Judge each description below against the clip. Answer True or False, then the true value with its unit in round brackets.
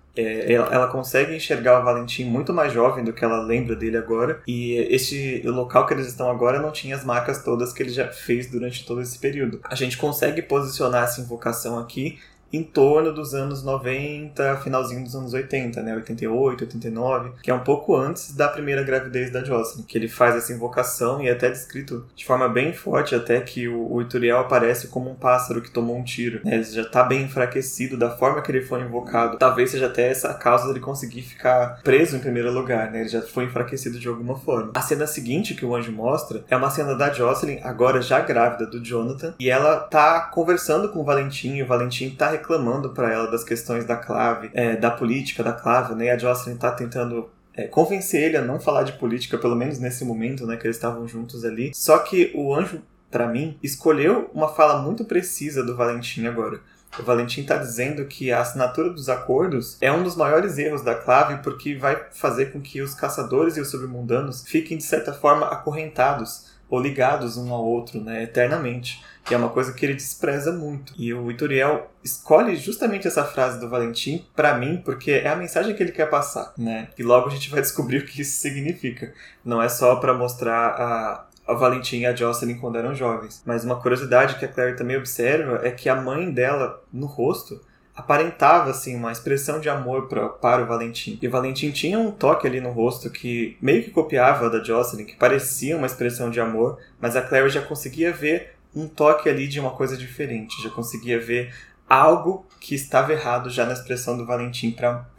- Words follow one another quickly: True (205 wpm)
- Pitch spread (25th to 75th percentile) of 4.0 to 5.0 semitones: False (2.8 semitones)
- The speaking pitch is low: True (125 Hz)